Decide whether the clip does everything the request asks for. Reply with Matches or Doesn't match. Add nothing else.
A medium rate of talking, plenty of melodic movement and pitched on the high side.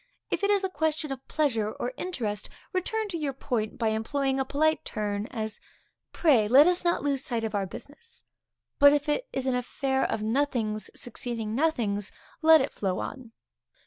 Matches